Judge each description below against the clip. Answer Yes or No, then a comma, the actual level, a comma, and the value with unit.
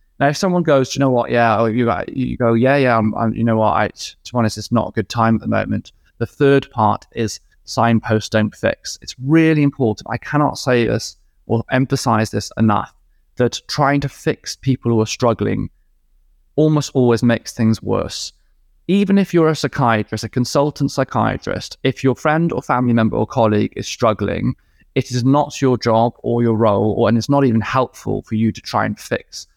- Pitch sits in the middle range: No, low, 115 Hz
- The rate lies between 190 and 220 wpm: Yes, average, 200 wpm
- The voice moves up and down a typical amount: Yes, average, 3.7 semitones